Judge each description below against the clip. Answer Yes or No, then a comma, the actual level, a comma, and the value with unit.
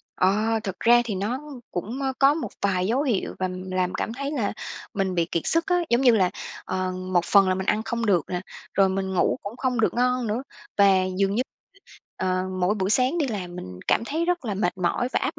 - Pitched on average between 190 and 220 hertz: Yes, high, 200 Hz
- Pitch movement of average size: Yes, average, 4.7 semitones